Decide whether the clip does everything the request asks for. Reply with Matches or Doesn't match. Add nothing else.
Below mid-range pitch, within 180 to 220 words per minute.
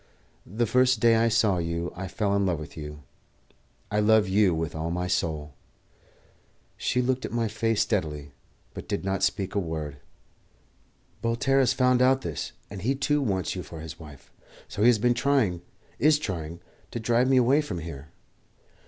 Matches